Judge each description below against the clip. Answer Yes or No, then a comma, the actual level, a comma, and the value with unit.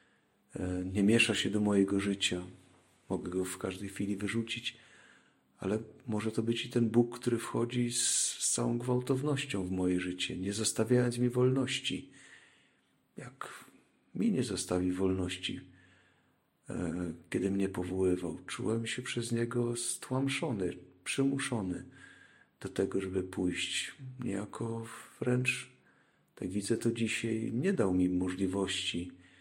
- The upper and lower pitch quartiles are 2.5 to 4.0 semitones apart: No, average, 4.5 semitones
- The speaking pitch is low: Yes, low, 105 Hz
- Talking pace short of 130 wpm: Yes, average, 120 wpm